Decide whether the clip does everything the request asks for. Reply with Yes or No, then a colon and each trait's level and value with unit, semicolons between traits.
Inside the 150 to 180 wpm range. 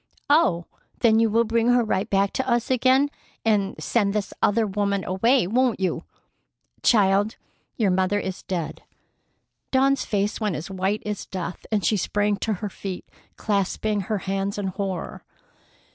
Yes: average, 160 wpm